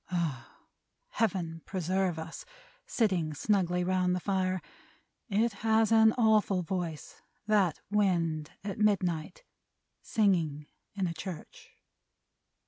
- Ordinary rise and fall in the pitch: Yes, average, 3.9 semitones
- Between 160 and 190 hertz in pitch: Yes, medium, 185 Hz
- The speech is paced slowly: Yes, slow, 105 wpm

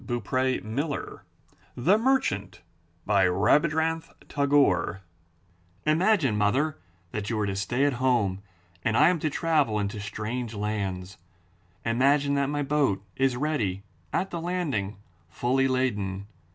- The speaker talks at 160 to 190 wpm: No, slow, 135 wpm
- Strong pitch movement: Yes, wide, 6.1 semitones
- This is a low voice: Yes, low, 125 Hz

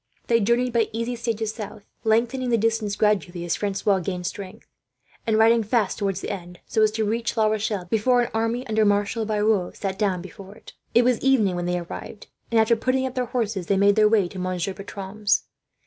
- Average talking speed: No, fast, 210 wpm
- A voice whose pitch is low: No, high, 215 Hz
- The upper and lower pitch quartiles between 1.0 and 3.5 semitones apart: Yes, average, 2.7 semitones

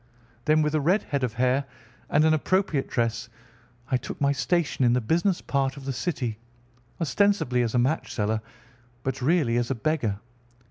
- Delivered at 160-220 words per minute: Yes, average, 180 wpm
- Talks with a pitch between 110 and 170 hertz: Yes, low, 135 Hz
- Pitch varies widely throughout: No, average, 4.3 semitones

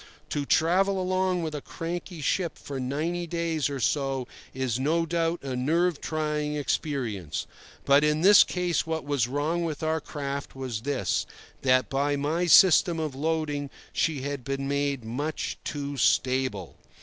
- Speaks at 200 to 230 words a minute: No, average, 155 wpm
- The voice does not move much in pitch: No, average, 3.3 semitones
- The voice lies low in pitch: No, medium, 145 Hz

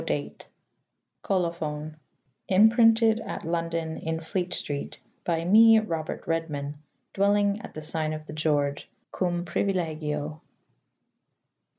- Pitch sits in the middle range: Yes, medium, 165 Hz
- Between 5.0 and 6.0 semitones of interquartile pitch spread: No, average, 4.1 semitones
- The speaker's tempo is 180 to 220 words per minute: No, average, 140 wpm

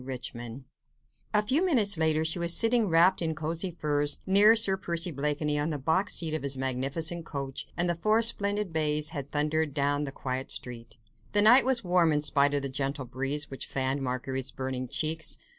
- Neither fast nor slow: Yes, average, 190 wpm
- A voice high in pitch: No, medium, 155 Hz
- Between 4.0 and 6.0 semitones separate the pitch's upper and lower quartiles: Yes, average, 4.4 semitones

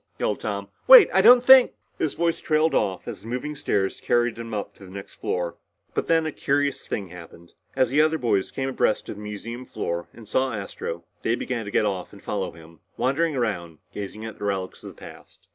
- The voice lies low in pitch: Yes, low, 115 Hz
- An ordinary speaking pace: No, fast, 220 wpm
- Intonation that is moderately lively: No, wide, 6.6 semitones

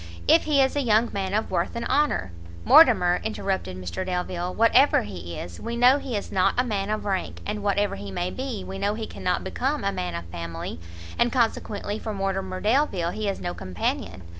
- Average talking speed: No, fast, 210 wpm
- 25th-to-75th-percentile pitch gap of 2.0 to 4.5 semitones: No, average, 4.9 semitones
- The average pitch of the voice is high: Yes, high, 195 Hz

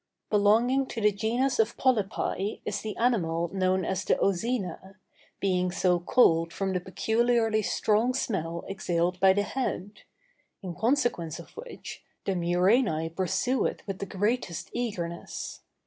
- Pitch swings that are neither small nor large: Yes, average, 4.4 semitones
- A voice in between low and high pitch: No, high, 200 Hz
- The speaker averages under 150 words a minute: Yes, average, 140 wpm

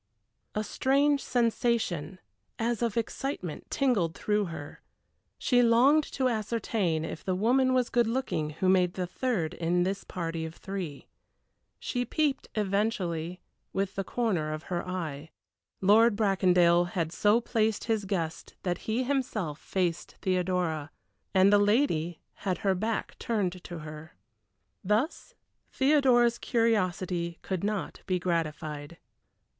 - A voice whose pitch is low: No, high, 195 Hz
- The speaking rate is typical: No, slow, 130 wpm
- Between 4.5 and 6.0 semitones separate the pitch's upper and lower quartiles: Yes, average, 5.2 semitones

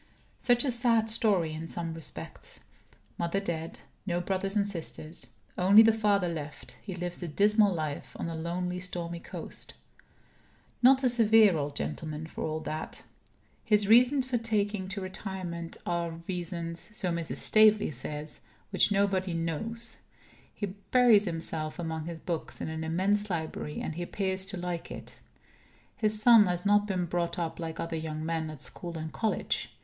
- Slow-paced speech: No, average, 165 wpm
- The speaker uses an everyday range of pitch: Yes, average, 4.1 semitones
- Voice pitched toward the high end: No, medium, 180 Hz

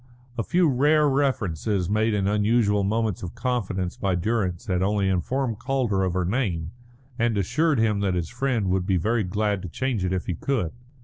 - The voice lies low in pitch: Yes, low, 105 Hz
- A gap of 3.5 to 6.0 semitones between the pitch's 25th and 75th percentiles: Yes, average, 4.5 semitones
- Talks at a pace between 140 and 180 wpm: No, average, 190 wpm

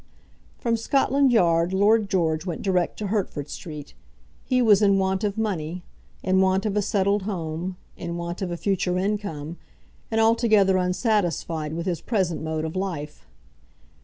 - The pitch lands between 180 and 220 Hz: Yes, high, 190 Hz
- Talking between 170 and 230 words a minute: No, average, 160 wpm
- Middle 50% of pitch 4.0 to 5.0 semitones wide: No, average, 3.6 semitones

